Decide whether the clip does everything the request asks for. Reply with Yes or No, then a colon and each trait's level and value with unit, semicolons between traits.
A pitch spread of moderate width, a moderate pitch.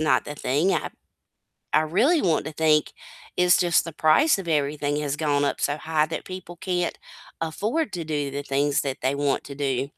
Yes: average, 3.4 semitones; medium, 155 Hz